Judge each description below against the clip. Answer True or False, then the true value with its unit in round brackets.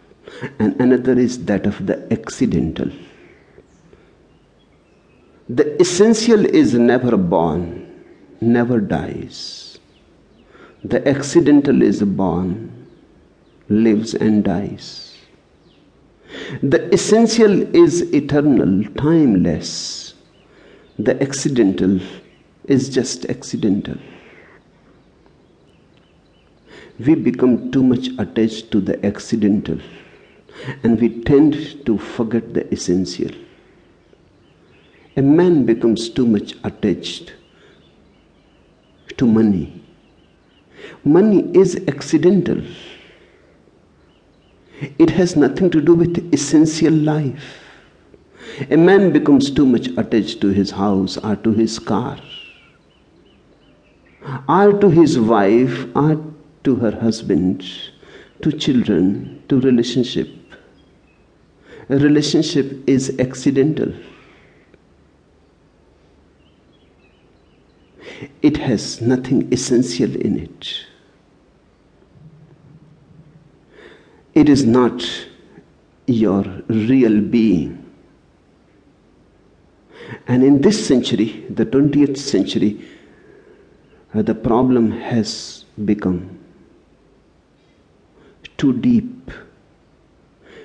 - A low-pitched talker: True (125 Hz)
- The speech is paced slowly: True (80 wpm)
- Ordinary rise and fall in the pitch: False (6.3 semitones)